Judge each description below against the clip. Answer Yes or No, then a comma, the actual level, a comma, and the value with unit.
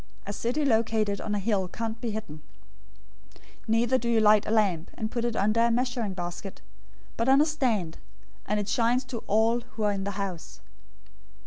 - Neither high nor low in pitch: No, high, 220 Hz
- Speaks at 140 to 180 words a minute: No, average, 195 wpm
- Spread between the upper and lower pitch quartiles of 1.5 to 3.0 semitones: Yes, average, 2.7 semitones